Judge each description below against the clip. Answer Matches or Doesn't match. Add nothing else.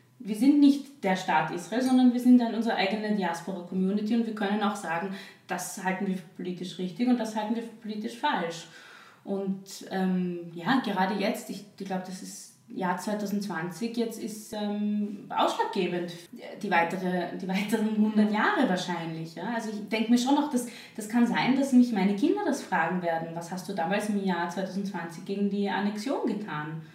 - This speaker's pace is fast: Doesn't match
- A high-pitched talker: Matches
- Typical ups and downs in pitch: Matches